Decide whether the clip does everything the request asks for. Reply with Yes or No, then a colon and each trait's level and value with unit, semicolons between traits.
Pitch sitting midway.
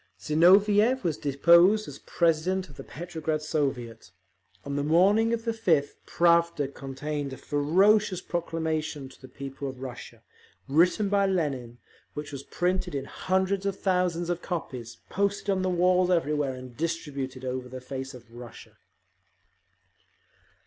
Yes: medium, 160 Hz